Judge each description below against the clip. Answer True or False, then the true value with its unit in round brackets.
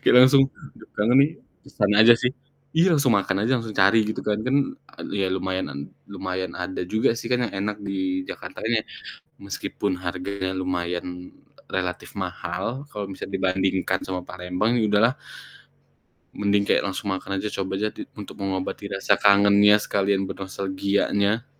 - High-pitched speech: False (100 Hz)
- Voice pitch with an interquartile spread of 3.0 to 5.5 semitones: False (2.5 semitones)